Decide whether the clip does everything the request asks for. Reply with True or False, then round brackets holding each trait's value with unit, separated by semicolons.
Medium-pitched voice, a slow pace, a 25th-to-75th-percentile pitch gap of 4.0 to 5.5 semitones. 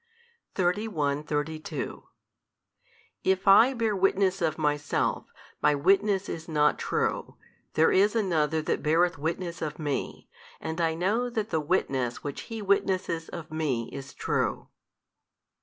True (165 Hz; 130 wpm; 4.4 semitones)